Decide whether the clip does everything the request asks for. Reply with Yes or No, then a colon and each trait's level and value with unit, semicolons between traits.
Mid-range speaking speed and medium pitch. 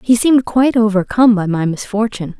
No: average, 175 wpm; high, 220 Hz